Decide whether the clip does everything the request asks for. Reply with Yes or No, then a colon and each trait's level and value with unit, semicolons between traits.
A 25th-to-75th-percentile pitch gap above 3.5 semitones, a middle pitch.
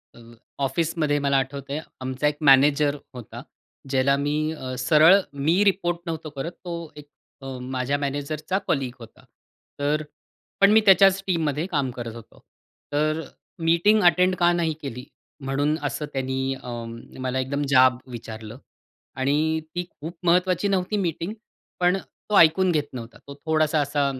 Yes: average, 4.1 semitones; medium, 150 Hz